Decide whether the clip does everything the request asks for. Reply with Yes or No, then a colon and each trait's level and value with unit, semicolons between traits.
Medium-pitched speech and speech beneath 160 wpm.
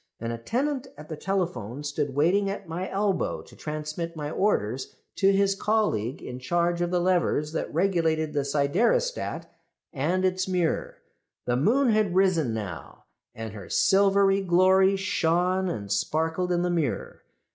Yes: medium, 175 Hz; average, 150 wpm